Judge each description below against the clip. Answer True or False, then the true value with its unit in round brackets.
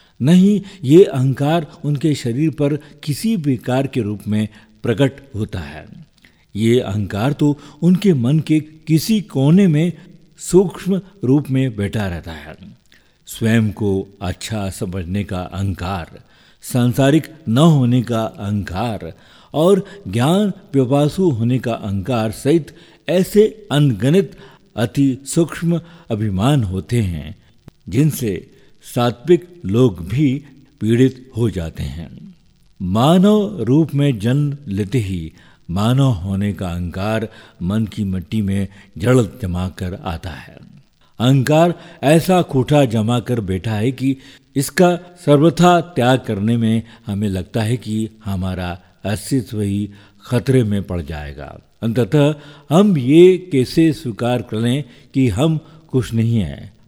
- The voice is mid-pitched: False (125 Hz)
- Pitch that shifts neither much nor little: False (6.6 semitones)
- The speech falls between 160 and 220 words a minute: False (120 wpm)